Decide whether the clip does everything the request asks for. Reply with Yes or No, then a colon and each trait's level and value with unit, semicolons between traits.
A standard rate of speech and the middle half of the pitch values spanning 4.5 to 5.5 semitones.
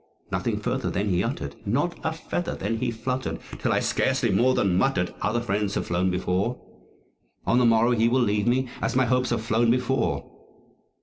No: average, 190 wpm; average, 4.0 semitones